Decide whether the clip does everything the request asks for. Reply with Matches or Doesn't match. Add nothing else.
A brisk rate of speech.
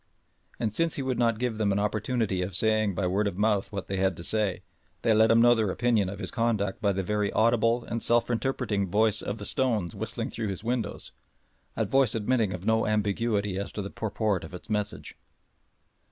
Matches